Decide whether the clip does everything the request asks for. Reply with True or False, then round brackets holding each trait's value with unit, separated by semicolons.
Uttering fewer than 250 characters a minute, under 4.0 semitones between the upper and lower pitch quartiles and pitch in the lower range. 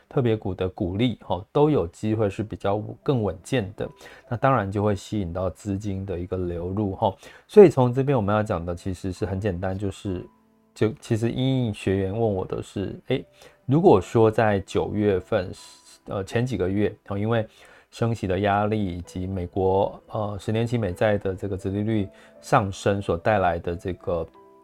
False (265 characters per minute; 2.9 semitones; 100 Hz)